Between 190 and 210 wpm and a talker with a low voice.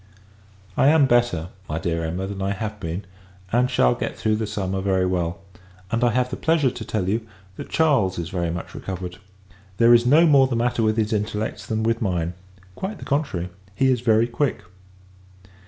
Yes: average, 195 wpm; low, 110 Hz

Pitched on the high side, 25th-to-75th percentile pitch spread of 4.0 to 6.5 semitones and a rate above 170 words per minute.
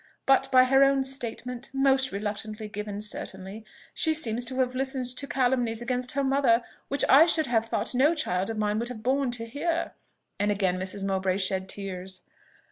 Yes: high, 240 Hz; average, 4.5 semitones; average, 185 wpm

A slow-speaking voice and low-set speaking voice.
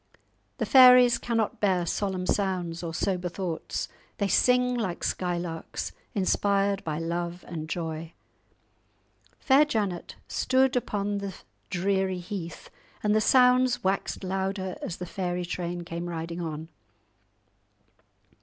No: slow, 120 wpm; medium, 185 Hz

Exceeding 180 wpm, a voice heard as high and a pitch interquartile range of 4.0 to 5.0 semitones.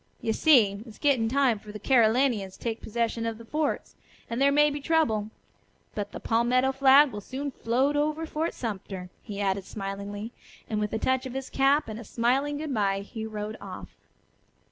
Yes: average, 190 wpm; high, 235 Hz; average, 4.7 semitones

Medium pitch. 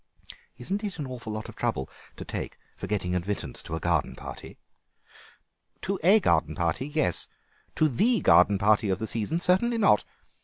No: low, 110 Hz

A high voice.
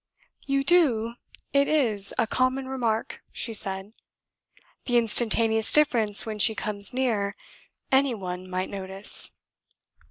Yes: high, 225 Hz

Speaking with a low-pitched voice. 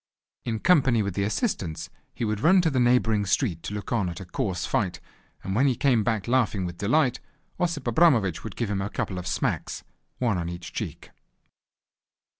Yes: low, 110 Hz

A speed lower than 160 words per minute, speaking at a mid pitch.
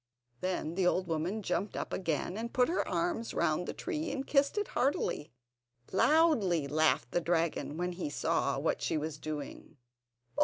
No: average, 165 wpm; medium, 180 Hz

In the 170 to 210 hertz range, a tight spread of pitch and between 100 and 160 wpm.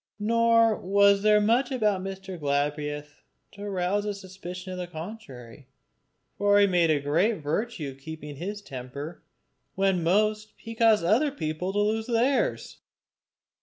No: high, 190 Hz; average, 5.3 semitones; average, 145 wpm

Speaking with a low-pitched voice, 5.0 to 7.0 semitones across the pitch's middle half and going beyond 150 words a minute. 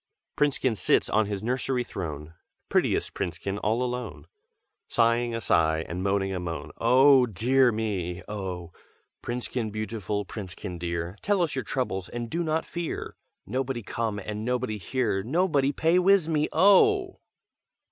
No: low, 115 Hz; wide, 5.6 semitones; average, 145 wpm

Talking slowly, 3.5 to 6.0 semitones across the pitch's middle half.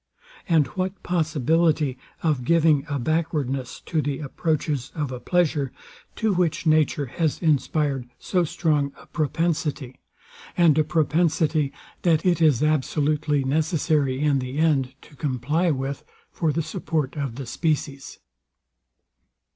No: slow, 130 wpm; average, 2.8 semitones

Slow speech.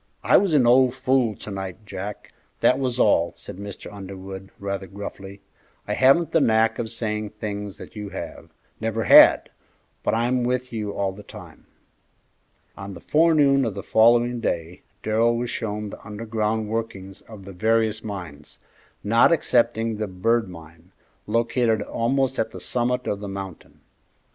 No: average, 160 wpm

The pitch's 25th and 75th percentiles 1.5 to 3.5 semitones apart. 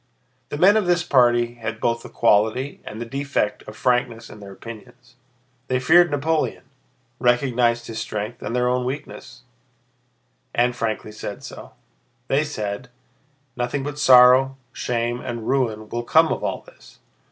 Yes: narrow, 2.6 semitones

